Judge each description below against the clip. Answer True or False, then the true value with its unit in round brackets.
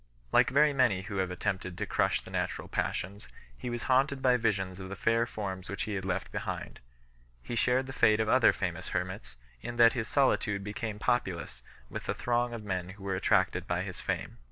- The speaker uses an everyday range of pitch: True (4.3 semitones)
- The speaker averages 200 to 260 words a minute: True (205 wpm)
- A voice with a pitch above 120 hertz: False (105 Hz)